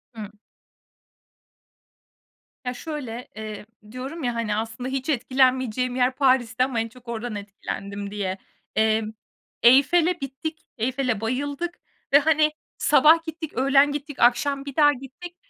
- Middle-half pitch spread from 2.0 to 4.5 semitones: Yes, average, 4.1 semitones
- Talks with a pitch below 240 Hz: No, very high, 255 Hz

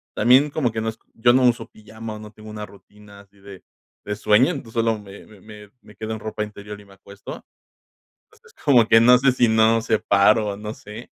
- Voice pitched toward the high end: No, low, 110 Hz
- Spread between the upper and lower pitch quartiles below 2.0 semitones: Yes, narrow, 1.6 semitones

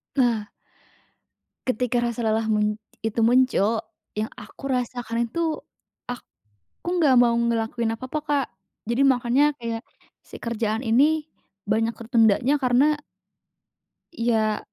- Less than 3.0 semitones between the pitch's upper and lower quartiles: Yes, narrow, 2.6 semitones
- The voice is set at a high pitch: Yes, high, 235 Hz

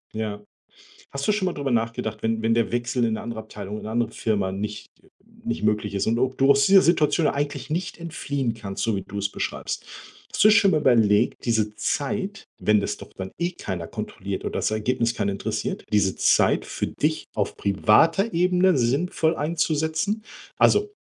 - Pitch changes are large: Yes, wide, 7.4 semitones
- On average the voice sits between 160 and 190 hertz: No, low, 120 Hz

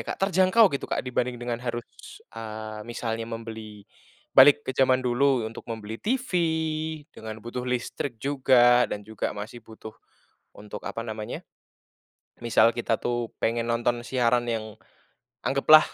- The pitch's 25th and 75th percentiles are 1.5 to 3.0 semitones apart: Yes, narrow, 2.4 semitones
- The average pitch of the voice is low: Yes, low, 120 Hz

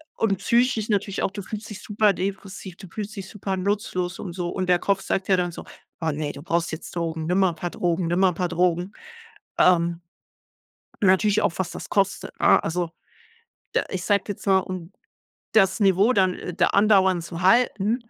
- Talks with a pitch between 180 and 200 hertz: Yes, high, 190 Hz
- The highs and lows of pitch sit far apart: No, narrow, 2.4 semitones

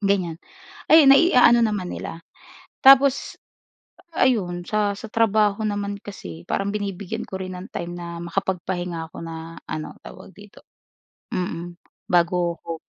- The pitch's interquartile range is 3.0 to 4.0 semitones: Yes, average, 3.7 semitones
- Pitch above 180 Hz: Yes, high, 190 Hz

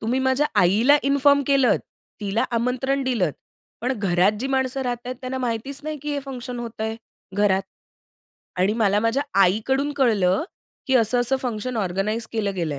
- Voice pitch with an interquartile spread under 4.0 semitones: No, average, 4.3 semitones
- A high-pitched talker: Yes, high, 240 Hz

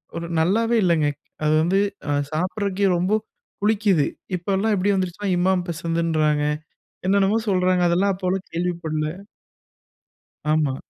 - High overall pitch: No, medium, 180 Hz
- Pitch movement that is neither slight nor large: Yes, average, 3.1 semitones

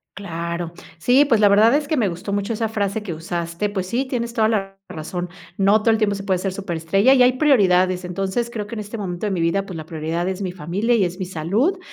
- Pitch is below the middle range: No, high, 195 Hz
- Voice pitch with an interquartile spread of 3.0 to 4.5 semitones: Yes, average, 4.0 semitones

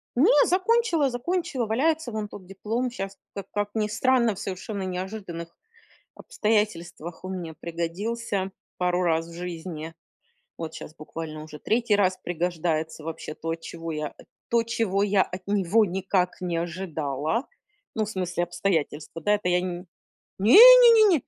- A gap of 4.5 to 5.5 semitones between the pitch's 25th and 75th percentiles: Yes, average, 4.9 semitones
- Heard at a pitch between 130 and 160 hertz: No, high, 190 Hz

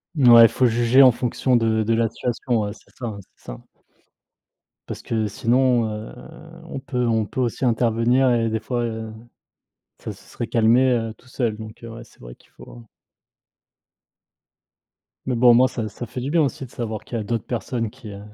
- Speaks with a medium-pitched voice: No, low, 115 Hz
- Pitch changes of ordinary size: No, narrow, 2.0 semitones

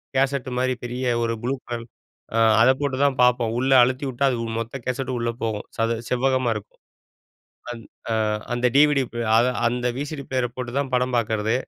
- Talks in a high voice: No, low, 125 Hz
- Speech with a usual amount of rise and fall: No, narrow, 1.9 semitones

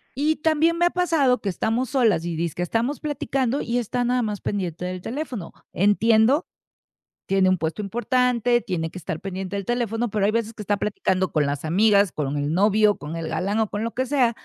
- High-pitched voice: Yes, high, 215 Hz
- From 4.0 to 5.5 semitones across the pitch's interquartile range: Yes, average, 5.0 semitones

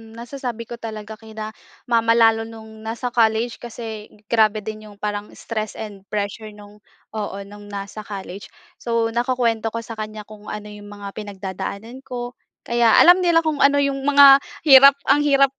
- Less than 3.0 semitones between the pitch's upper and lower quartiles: Yes, narrow, 2.4 semitones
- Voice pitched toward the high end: Yes, high, 225 Hz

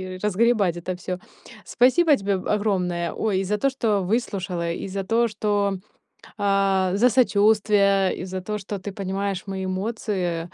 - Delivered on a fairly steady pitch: Yes, narrow, 2.2 semitones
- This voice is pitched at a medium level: No, high, 200 Hz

